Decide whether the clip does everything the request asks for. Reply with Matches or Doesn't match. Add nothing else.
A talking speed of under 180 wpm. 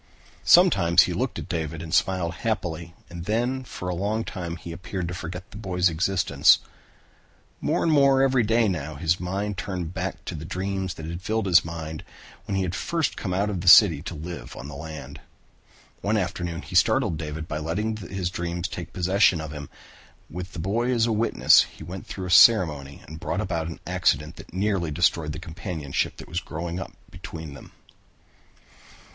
Doesn't match